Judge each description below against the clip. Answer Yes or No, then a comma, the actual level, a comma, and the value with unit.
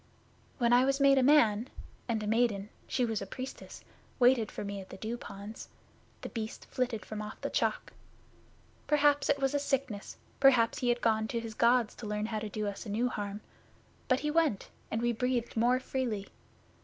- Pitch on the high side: Yes, high, 235 Hz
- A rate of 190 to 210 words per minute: Yes, average, 195 wpm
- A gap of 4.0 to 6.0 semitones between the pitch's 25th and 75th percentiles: No, average, 3.3 semitones